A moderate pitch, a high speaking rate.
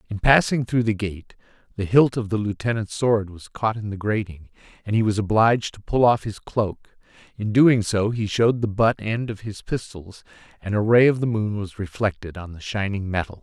No: low, 105 Hz; fast, 215 wpm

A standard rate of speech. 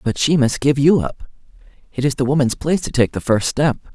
No: fast, 245 wpm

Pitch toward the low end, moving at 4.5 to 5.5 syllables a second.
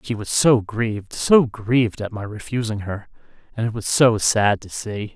Yes: low, 110 Hz; 4.9 syllables/s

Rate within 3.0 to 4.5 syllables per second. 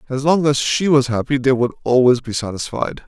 No: 5.5 syllables/s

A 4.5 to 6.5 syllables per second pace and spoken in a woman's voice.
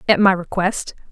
Yes: 5.0 syllables/s; female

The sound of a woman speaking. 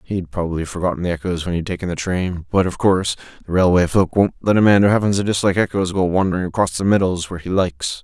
No: male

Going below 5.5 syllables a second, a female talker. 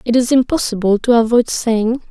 Yes: 5.1 syllables/s; female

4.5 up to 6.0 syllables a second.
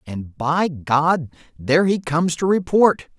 No: 4.1 syllables/s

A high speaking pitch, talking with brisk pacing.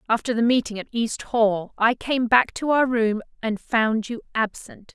No: high, 230 Hz; average, 195 wpm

